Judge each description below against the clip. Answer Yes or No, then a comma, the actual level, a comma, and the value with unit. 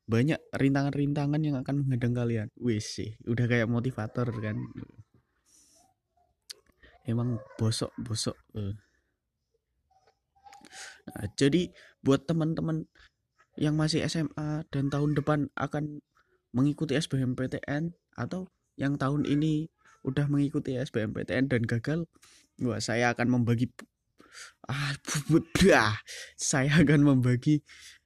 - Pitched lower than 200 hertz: Yes, medium, 140 Hz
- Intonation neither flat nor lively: Yes, average, 3.9 semitones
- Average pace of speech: Yes, average, 100 wpm